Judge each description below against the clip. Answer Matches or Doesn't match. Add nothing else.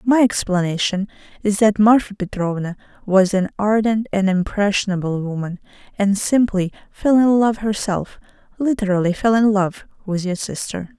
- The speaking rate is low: Matches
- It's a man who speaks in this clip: Doesn't match